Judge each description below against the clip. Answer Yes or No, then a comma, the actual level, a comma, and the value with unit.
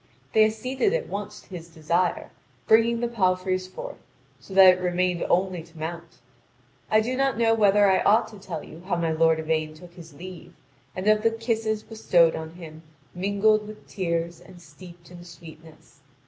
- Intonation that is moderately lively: Yes, average, 4.2 semitones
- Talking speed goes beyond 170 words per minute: Yes, average, 180 wpm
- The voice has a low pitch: No, medium, 185 Hz